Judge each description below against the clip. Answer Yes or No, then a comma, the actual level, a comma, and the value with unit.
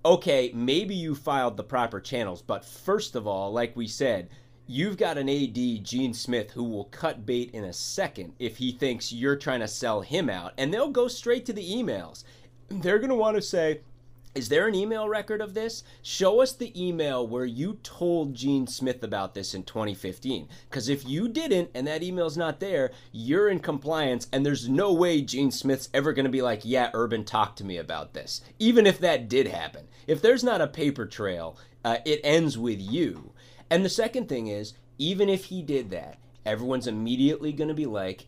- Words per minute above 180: Yes, fast, 205 wpm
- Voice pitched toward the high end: No, low, 135 Hz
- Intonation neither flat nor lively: No, wide, 5.8 semitones